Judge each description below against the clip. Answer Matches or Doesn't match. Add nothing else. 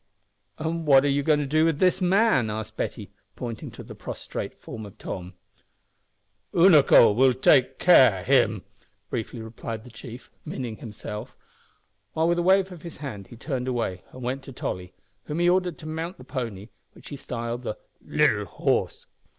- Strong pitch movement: Matches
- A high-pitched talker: Doesn't match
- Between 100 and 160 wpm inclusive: Doesn't match